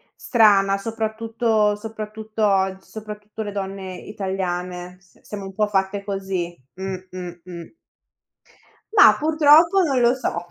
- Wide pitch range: No, narrow, 2.5 semitones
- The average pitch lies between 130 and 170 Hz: No, high, 205 Hz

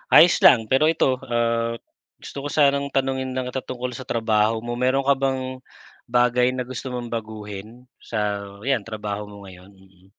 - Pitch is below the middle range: Yes, low, 120 Hz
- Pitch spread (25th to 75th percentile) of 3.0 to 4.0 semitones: Yes, average, 3.5 semitones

